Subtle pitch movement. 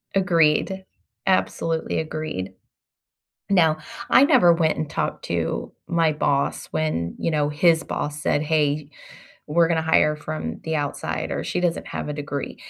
Yes: narrow, 2.2 semitones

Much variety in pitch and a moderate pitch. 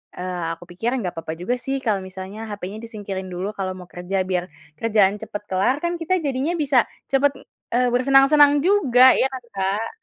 No: wide, 6.2 semitones; high, 215 Hz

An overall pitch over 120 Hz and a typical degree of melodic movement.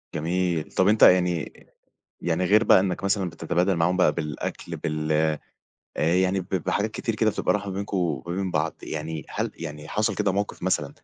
No: very low, 90 Hz; average, 3.1 semitones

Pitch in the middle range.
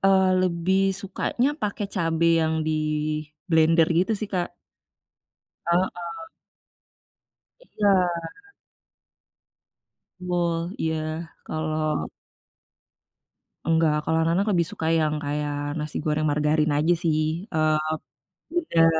Yes: medium, 160 Hz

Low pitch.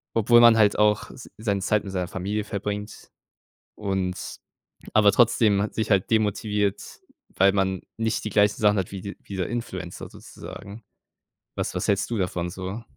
Yes: low, 100 Hz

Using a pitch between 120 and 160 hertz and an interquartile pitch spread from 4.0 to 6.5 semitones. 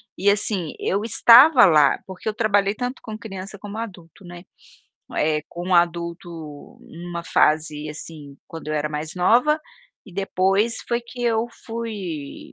No: high, 190 Hz; average, 5.0 semitones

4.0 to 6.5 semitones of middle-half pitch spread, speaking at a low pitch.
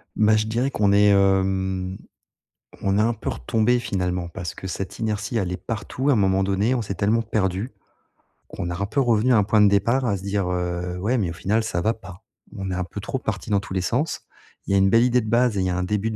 No: average, 2.9 semitones; low, 100 Hz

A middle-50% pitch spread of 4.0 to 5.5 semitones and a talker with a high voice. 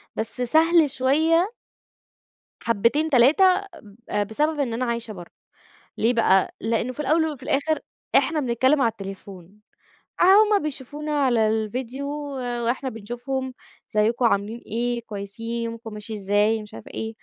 Yes: average, 4.4 semitones; high, 240 Hz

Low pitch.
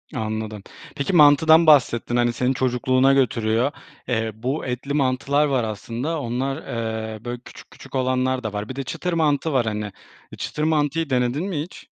Yes: low, 130 Hz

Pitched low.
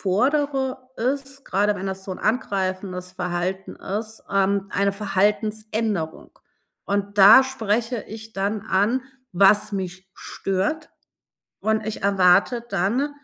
No: high, 205 Hz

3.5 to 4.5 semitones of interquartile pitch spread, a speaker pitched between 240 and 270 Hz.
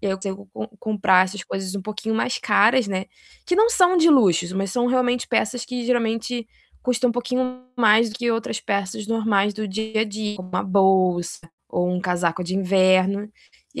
No: average, 4.1 semitones; high, 210 Hz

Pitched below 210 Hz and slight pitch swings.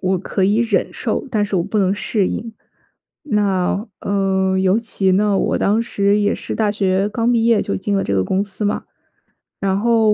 Yes: high, 200 Hz; narrow, 2.2 semitones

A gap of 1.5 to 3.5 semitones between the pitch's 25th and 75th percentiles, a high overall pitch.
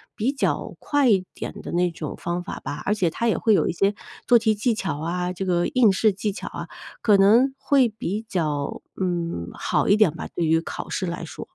No: average, 4.2 semitones; high, 195 Hz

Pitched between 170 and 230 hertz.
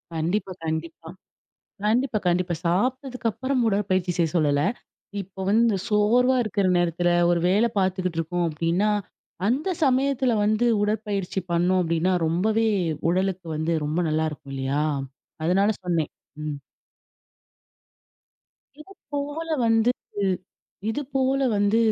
Yes: high, 190 Hz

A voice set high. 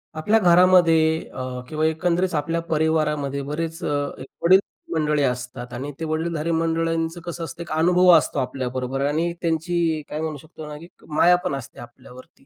No: medium, 160 Hz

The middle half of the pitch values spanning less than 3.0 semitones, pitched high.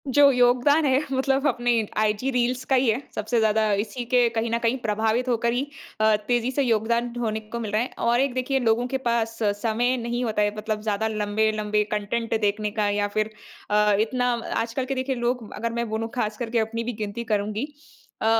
Yes: narrow, 2.4 semitones; high, 230 Hz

